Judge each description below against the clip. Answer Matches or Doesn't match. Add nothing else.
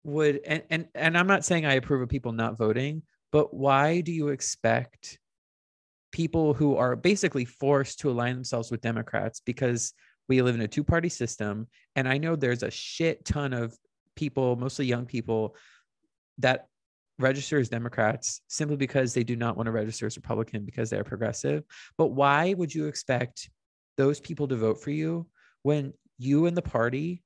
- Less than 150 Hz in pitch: Matches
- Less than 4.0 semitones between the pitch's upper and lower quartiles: Doesn't match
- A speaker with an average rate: Matches